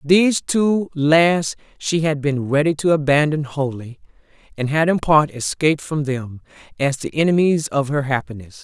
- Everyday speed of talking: Yes, average, 160 wpm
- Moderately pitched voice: Yes, medium, 150 Hz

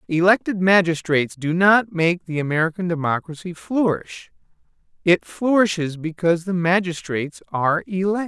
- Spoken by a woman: No, male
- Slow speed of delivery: Yes, slow, 115 wpm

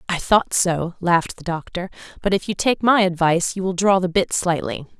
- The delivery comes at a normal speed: No, fast, 215 wpm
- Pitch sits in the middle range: Yes, medium, 180 Hz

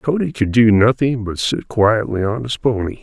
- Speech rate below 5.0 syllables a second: Yes, 4.7 syllables/s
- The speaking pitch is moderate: No, low, 115 Hz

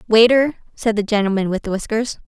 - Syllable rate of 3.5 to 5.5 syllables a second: No, 6.0 syllables/s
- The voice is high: Yes, high, 220 Hz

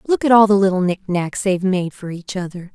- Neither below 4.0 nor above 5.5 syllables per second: No, 5.9 syllables/s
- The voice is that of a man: No, female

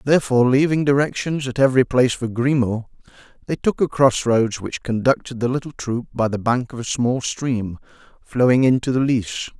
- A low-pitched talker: Yes, low, 125 Hz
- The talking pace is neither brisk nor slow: Yes, average, 175 wpm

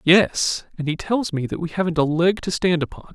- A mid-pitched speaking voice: Yes, medium, 170 Hz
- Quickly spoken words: Yes, fast, 250 wpm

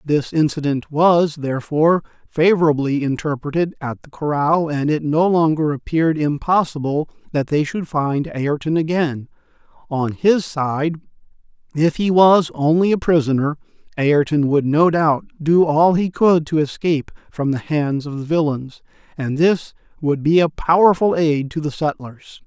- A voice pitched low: No, medium, 155 Hz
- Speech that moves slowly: No, average, 150 wpm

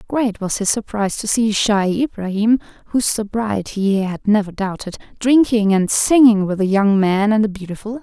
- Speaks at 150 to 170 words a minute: No, average, 185 wpm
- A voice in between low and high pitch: No, high, 210 Hz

